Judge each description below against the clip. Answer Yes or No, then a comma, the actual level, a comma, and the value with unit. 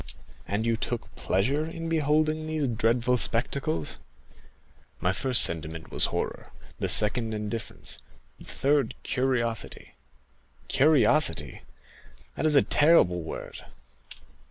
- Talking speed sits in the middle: No, slow, 105 wpm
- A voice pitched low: Yes, low, 120 Hz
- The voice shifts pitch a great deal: Yes, wide, 6.0 semitones